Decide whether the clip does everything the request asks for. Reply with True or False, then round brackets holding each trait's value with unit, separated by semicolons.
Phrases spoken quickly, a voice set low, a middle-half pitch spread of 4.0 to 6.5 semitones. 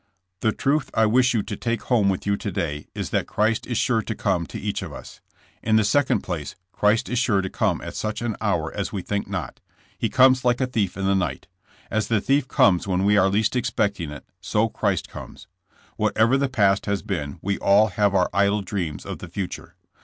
False (225 wpm; 105 Hz; 2.9 semitones)